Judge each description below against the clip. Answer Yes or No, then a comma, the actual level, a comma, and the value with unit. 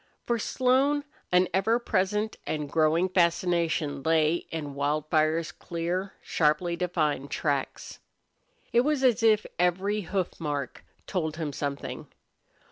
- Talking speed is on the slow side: Yes, slow, 120 wpm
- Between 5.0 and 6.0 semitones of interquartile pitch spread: No, average, 4.4 semitones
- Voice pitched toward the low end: No, medium, 170 Hz